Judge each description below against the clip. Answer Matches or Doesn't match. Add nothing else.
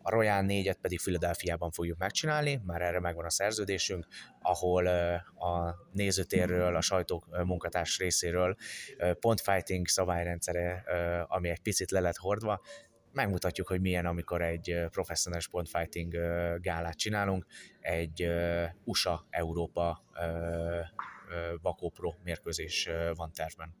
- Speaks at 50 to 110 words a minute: Matches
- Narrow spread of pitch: Matches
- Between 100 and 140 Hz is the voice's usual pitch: Doesn't match